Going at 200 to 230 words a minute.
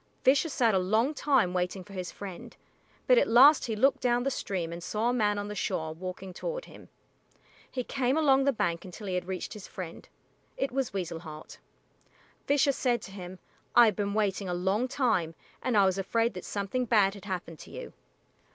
Yes: fast, 205 wpm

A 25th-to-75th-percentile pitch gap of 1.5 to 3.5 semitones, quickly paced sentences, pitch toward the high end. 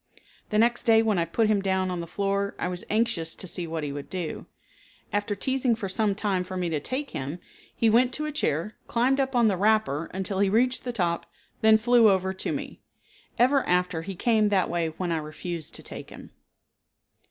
No: average, 4.4 semitones; fast, 215 wpm; high, 200 Hz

